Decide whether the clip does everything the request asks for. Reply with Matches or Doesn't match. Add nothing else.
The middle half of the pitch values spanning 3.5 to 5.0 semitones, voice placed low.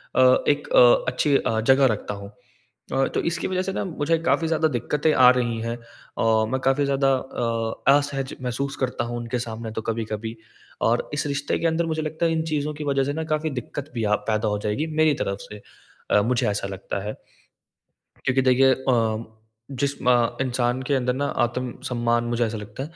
Matches